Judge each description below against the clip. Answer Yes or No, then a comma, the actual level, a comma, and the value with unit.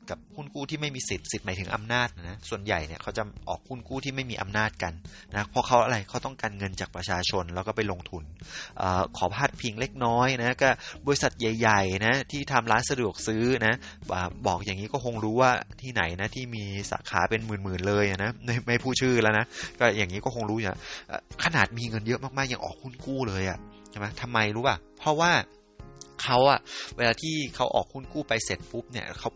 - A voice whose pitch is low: Yes, low, 110 Hz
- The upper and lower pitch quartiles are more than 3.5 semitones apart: Yes, average, 4.0 semitones